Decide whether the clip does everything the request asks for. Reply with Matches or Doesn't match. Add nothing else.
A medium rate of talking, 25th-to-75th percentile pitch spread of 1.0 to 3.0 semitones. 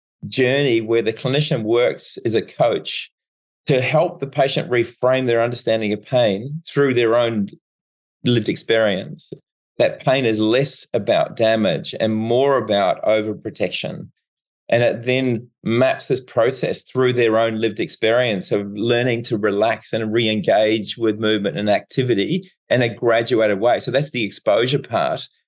Matches